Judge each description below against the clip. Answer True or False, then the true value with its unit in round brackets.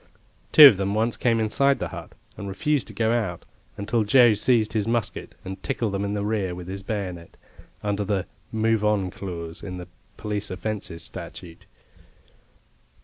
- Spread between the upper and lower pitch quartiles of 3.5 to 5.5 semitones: False (3.0 semitones)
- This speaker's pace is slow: False (170 wpm)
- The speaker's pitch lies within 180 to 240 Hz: False (105 Hz)